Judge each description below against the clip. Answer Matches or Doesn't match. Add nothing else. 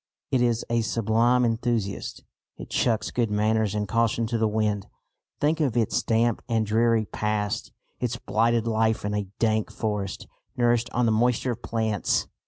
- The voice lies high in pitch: Doesn't match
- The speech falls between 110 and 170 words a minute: Matches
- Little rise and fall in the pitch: Matches